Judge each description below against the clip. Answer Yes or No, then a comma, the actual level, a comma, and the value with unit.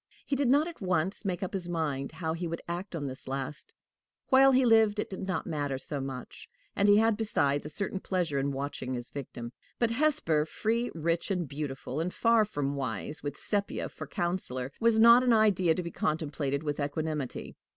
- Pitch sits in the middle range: Yes, medium, 165 Hz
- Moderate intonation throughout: No, wide, 6.5 semitones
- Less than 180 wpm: No, average, 200 wpm